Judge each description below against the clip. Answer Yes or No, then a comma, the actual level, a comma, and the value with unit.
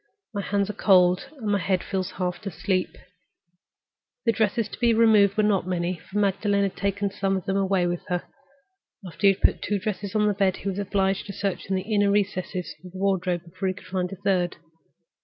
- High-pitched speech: Yes, high, 195 Hz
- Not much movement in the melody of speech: Yes, narrow, 1.7 semitones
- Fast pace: Yes, fast, 215 wpm